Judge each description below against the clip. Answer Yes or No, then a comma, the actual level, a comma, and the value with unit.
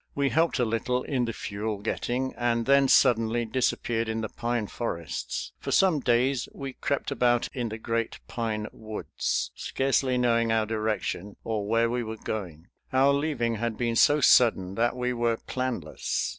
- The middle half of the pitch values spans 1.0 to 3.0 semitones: Yes, narrow, 2.4 semitones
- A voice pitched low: Yes, low, 115 Hz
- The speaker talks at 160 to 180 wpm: Yes, average, 170 wpm